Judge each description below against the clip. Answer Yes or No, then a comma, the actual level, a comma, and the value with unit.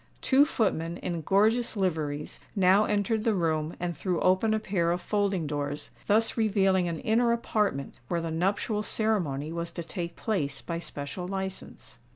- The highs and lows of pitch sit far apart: No, average, 4.2 semitones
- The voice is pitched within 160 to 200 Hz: Yes, medium, 185 Hz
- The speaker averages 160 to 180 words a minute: Yes, average, 165 wpm